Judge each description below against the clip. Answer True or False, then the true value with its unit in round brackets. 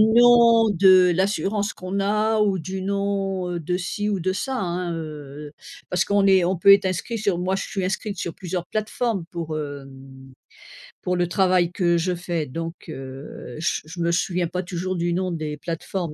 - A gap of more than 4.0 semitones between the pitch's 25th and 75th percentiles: False (2.8 semitones)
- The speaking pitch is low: False (180 Hz)